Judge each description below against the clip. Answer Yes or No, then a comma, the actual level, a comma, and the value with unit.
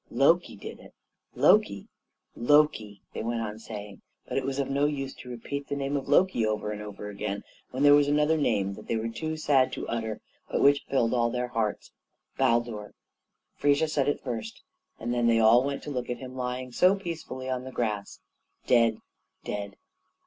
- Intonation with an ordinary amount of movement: Yes, average, 4.2 semitones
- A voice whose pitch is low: Yes, low, 125 Hz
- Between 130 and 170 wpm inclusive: No, average, 190 wpm